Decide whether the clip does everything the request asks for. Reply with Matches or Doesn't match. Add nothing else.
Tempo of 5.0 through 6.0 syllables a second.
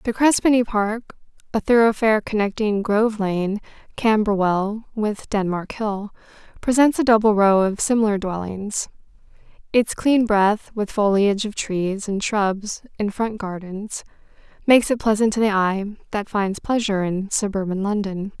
Doesn't match